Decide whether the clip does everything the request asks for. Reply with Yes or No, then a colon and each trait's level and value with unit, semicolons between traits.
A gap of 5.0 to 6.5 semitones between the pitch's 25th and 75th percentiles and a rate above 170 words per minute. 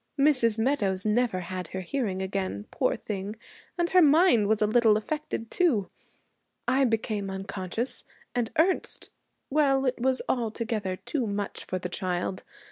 No: wide, 5.5 semitones; average, 145 wpm